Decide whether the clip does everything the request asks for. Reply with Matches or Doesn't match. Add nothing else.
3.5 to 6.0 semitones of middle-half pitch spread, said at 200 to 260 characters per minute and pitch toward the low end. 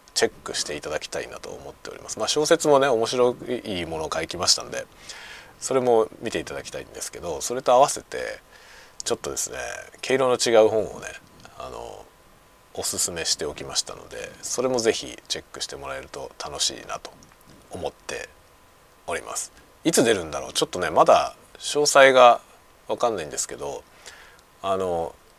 Doesn't match